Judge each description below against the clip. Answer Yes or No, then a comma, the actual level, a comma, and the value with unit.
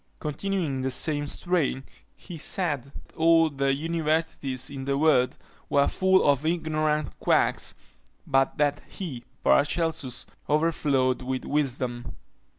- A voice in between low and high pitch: Yes, medium, 145 Hz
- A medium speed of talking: No, slow, 120 wpm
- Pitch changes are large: No, average, 3.3 semitones